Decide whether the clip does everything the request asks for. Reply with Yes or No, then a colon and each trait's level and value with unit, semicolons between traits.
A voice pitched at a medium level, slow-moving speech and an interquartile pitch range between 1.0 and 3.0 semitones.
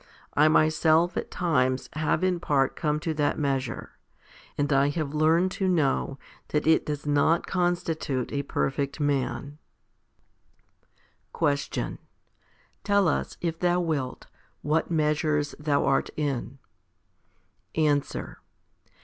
Yes: medium, 150 Hz; slow, 120 wpm; narrow, 2.4 semitones